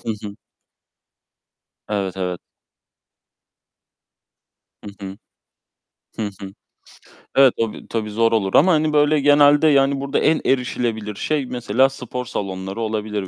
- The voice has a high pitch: No, low, 115 Hz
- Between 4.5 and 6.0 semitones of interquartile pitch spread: Yes, average, 5.2 semitones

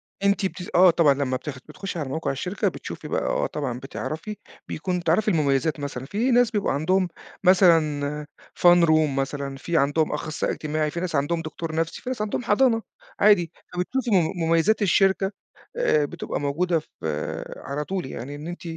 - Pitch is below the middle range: No, medium, 165 Hz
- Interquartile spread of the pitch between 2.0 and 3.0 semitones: No, average, 4.5 semitones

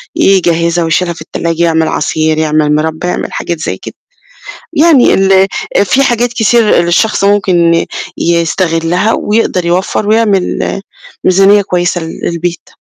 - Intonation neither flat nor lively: Yes, average, 3.4 semitones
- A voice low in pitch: No, medium, 175 Hz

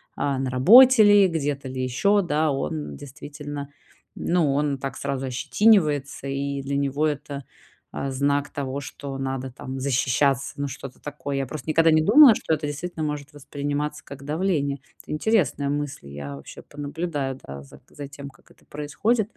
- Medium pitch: Yes, medium, 145 Hz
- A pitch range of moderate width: No, narrow, 2.2 semitones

